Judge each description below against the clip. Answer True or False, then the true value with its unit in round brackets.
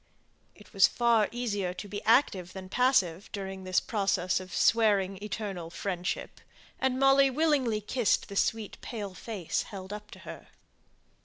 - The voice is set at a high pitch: True (205 Hz)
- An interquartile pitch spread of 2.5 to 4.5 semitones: True (3.7 semitones)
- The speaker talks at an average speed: True (150 wpm)